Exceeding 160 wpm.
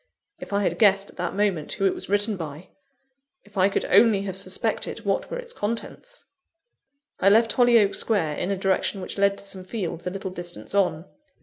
Yes: average, 200 wpm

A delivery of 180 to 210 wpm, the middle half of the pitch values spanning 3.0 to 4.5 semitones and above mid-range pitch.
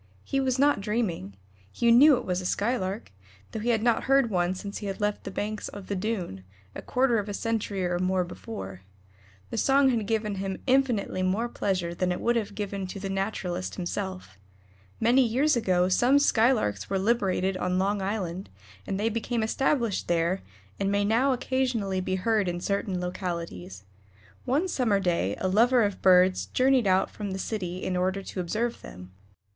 Yes: average, 185 wpm; average, 4.1 semitones; high, 200 Hz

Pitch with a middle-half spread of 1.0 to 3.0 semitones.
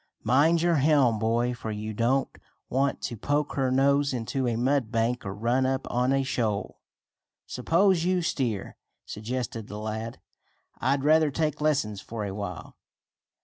No: average, 4.1 semitones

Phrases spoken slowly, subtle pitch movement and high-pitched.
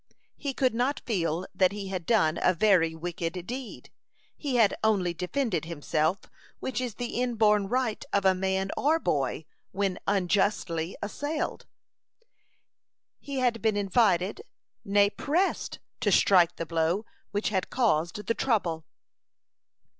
No: slow, 130 wpm; average, 5.2 semitones; high, 200 Hz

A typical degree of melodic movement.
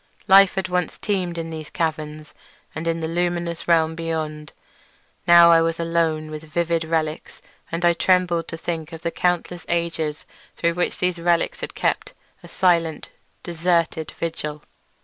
No: narrow, 1.4 semitones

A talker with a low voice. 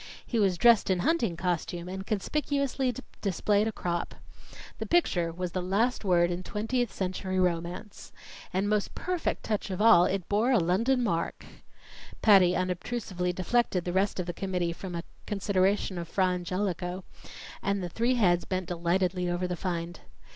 No: medium, 185 Hz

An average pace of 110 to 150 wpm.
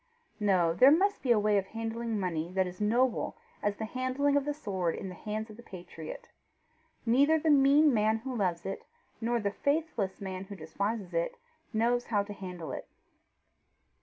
No: average, 185 wpm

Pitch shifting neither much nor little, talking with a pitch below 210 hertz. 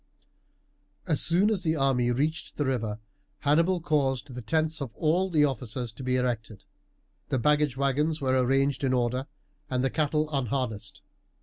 Yes: average, 3.5 semitones; low, 135 Hz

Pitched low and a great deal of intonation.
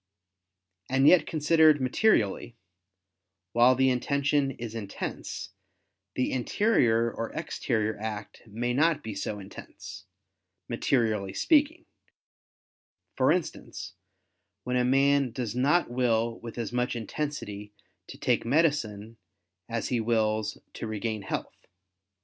No: low, 120 Hz; average, 4.2 semitones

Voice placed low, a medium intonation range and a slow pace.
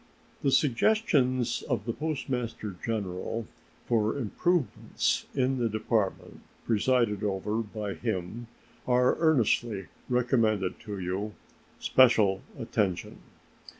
Yes: low, 115 Hz; average, 3.5 semitones; slow, 95 wpm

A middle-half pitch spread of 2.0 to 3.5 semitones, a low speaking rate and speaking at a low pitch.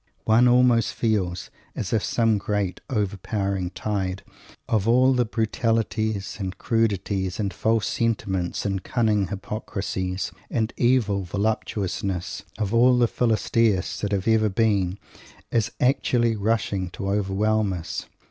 Yes: average, 2.8 semitones; slow, 125 wpm; low, 105 Hz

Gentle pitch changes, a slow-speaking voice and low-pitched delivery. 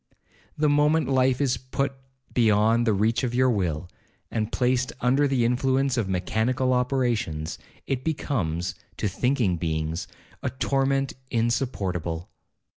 No: average, 5.2 semitones; slow, 125 wpm; low, 125 Hz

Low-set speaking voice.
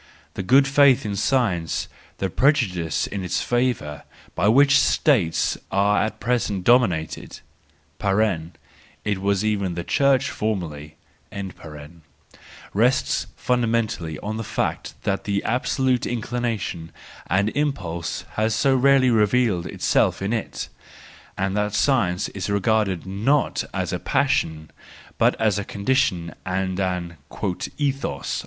Yes: low, 105 Hz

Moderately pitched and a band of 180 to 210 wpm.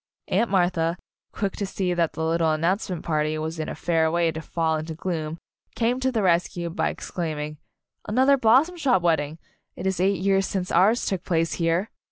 Yes: medium, 175 Hz; fast, 205 wpm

